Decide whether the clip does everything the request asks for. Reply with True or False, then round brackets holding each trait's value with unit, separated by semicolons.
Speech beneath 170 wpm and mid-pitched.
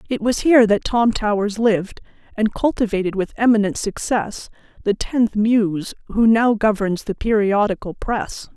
False (145 wpm; 215 Hz)